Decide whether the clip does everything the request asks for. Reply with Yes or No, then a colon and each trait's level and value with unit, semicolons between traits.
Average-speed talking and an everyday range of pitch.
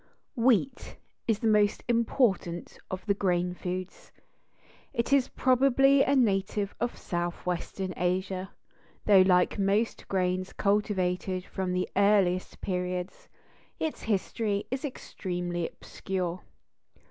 No: slow, 110 wpm; average, 3.7 semitones